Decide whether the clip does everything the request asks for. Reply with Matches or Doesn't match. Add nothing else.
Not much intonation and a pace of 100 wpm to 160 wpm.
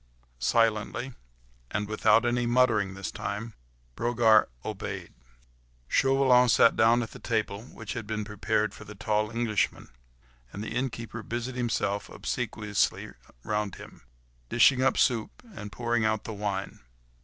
Matches